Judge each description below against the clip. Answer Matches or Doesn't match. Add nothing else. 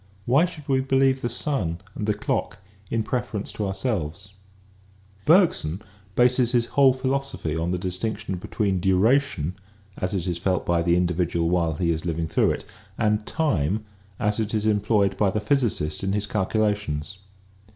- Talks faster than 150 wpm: Matches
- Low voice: Matches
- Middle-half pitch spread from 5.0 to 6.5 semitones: Matches